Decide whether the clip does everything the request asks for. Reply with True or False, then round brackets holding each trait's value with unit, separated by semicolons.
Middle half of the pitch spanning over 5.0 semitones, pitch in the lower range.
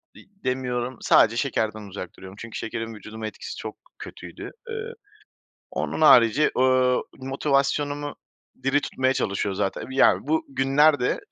False (3.9 semitones; 130 Hz)